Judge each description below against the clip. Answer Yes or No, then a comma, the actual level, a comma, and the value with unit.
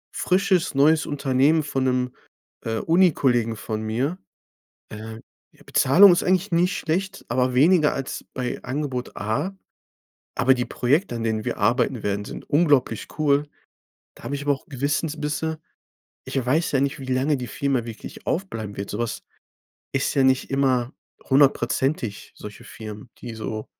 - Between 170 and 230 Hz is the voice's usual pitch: No, low, 135 Hz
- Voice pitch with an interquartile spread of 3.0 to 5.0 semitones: Yes, average, 4.2 semitones